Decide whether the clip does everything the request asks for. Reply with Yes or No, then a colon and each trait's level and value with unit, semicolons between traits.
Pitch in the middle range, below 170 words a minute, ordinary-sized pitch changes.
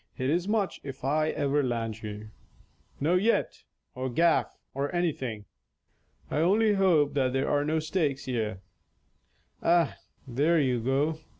Yes: medium, 145 Hz; average, 140 wpm; average, 4.5 semitones